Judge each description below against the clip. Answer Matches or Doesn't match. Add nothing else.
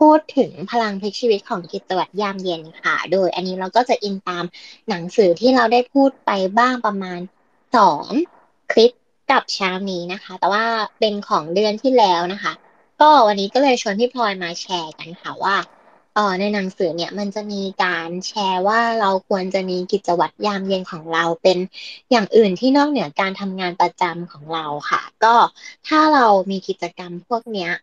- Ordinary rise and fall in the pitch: Matches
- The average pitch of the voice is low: Doesn't match